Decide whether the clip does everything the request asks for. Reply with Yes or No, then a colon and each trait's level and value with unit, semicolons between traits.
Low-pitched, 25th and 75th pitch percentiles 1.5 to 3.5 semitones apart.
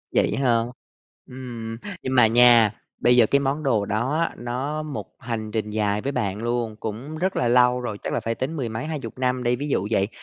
Yes: low, 120 Hz; average, 2.9 semitones